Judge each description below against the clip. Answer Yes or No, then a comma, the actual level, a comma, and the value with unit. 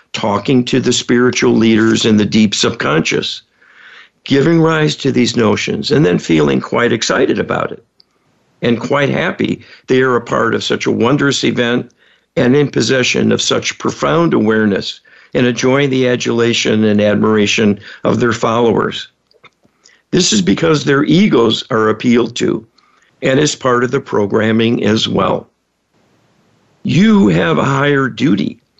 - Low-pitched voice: Yes, low, 120 Hz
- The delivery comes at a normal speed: Yes, average, 145 wpm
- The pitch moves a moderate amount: Yes, average, 4.0 semitones